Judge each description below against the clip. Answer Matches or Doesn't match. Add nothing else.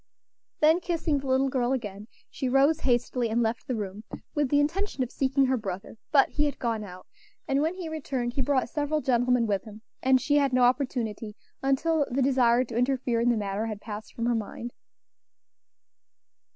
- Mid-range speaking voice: Doesn't match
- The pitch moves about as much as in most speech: Matches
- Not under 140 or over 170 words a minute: Doesn't match